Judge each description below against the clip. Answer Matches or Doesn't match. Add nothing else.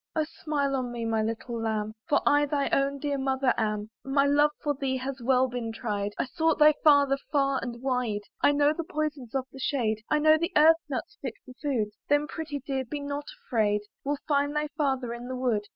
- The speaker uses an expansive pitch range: Doesn't match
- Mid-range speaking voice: Doesn't match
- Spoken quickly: Matches